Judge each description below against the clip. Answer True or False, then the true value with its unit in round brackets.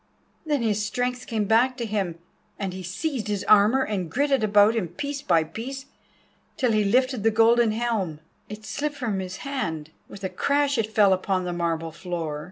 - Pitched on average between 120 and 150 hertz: False (215 Hz)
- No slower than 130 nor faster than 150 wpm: False (190 wpm)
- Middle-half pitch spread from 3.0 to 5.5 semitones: True (5.0 semitones)